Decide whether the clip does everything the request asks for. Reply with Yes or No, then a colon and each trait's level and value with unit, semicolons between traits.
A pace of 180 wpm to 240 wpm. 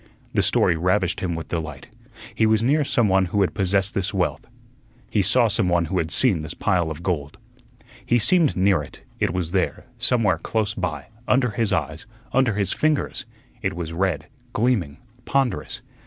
No: average, 170 wpm